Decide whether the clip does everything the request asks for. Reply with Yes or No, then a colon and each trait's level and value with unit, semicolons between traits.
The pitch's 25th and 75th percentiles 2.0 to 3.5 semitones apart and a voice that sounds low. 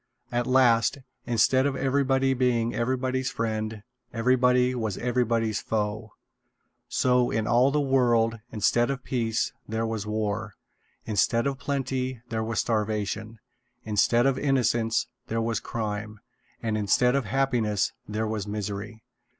Yes: average, 2.7 semitones; low, 115 Hz